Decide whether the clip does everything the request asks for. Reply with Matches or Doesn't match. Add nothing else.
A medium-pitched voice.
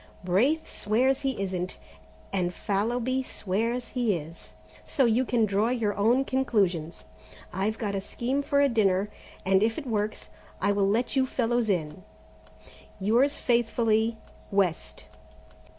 Doesn't match